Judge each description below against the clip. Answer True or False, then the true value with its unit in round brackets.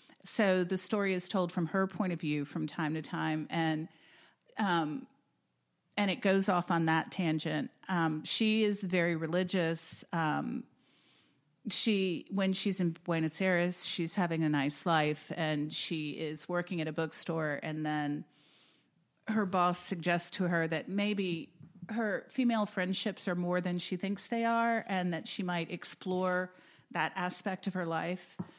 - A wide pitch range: False (3.0 semitones)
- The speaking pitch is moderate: True (180 Hz)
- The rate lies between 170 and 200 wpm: False (160 wpm)